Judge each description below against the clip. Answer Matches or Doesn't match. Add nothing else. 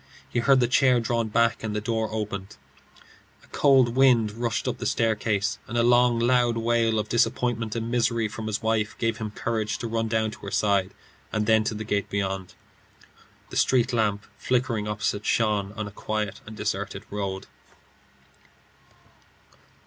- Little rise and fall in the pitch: Matches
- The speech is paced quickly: Doesn't match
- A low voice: Matches